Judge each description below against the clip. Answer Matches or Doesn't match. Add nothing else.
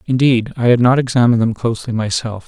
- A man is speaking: Matches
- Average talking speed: Matches